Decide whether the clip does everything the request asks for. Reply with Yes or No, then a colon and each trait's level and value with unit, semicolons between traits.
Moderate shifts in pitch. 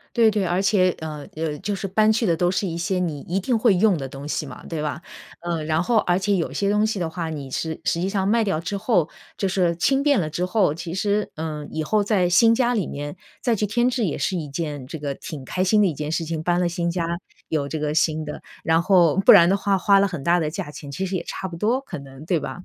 Yes: average, 4.2 semitones